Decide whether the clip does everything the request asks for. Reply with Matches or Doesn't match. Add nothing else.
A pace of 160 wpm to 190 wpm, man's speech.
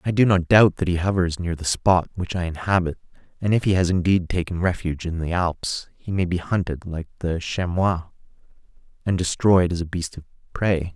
Doesn't match